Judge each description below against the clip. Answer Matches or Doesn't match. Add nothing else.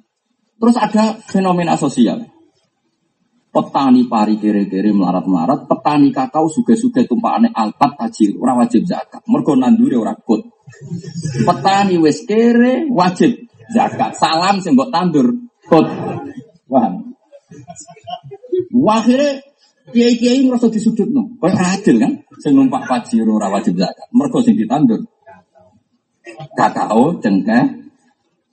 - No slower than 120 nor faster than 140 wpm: Doesn't match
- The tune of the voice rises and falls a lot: Matches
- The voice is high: Matches